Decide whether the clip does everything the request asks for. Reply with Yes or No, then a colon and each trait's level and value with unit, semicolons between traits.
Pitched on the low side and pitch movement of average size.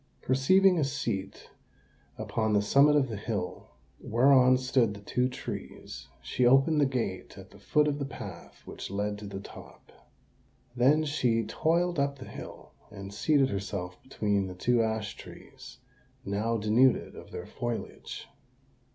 Yes: low, 125 Hz; average, 5.0 semitones